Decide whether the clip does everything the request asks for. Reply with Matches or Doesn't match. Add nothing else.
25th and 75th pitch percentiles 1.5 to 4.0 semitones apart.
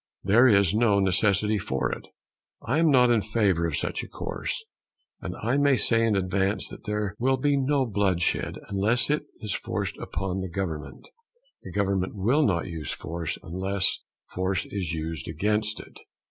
Matches